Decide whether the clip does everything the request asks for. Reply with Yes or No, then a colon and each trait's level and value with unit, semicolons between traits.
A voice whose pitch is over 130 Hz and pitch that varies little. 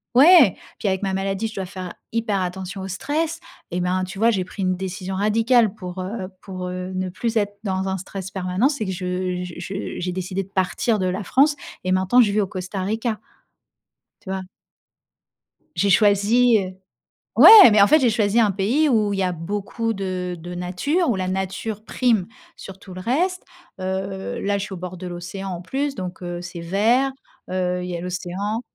No: high, 190 Hz; average, 3.0 semitones